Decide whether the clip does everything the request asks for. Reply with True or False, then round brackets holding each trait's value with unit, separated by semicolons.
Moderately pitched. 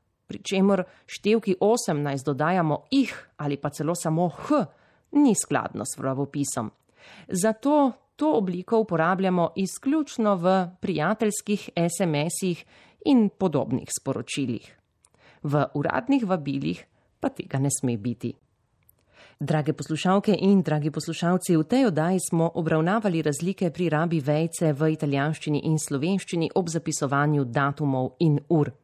True (165 Hz)